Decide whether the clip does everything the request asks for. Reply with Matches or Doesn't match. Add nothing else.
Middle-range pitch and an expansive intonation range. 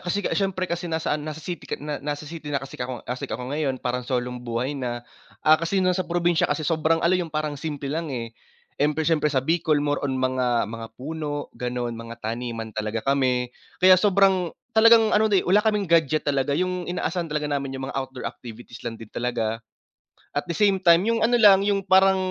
Matches